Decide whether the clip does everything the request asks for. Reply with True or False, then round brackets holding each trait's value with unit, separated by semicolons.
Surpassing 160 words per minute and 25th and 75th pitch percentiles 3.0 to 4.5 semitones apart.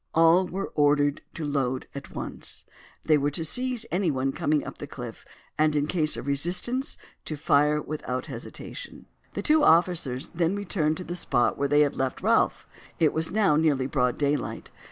True (175 wpm; 3.7 semitones)